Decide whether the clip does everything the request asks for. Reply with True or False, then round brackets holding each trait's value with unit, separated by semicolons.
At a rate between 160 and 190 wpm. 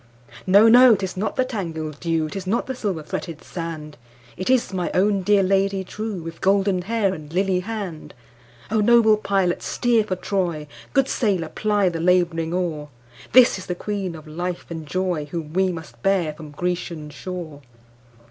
False (150 wpm)